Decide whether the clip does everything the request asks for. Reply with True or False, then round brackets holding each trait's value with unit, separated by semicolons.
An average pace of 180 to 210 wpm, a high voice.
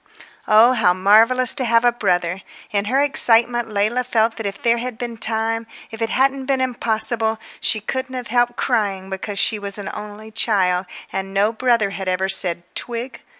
True (185 wpm; 225 Hz)